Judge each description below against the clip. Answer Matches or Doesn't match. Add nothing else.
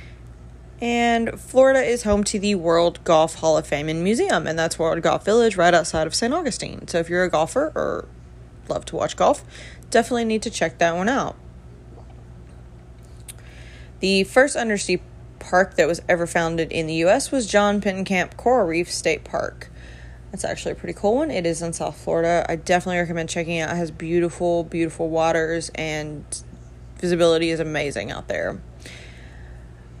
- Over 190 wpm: Doesn't match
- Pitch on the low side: Doesn't match